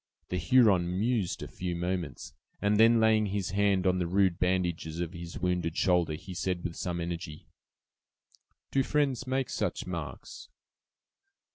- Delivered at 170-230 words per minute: No, average, 150 wpm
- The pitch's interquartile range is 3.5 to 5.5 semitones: No, average, 3.1 semitones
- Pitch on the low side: Yes, very low, 90 Hz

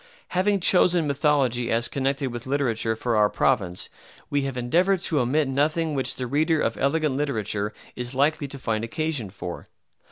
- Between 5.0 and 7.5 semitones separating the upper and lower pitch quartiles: No, average, 4.6 semitones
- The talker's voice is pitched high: No, low, 135 Hz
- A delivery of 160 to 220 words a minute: Yes, average, 165 wpm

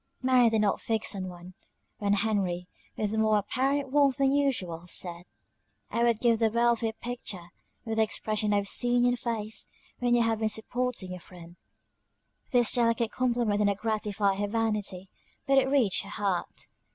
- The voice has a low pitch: No, high, 220 Hz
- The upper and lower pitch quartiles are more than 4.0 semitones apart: No, average, 3.2 semitones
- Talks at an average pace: Yes, average, 185 wpm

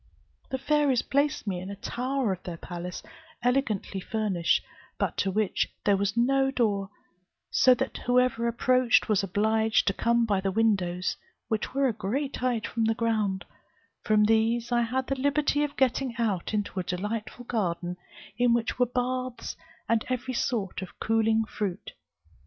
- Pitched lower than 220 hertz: No, high, 225 Hz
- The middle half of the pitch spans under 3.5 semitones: No, average, 3.9 semitones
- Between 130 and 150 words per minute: No, average, 165 wpm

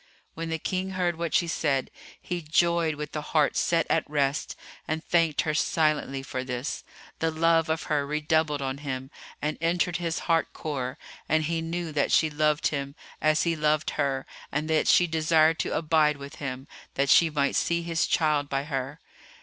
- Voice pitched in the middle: Yes, medium, 155 Hz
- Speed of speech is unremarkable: Yes, average, 185 wpm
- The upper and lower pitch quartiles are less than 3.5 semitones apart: Yes, narrow, 2.5 semitones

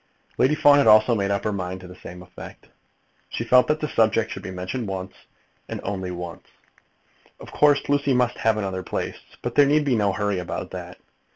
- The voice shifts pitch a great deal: Yes, wide, 5.9 semitones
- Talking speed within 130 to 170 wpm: No, fast, 205 wpm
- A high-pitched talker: No, low, 110 Hz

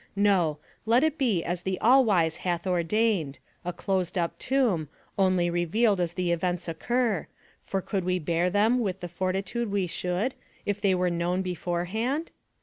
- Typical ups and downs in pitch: Yes, average, 3.6 semitones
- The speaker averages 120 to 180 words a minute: Yes, average, 165 wpm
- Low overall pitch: No, medium, 185 Hz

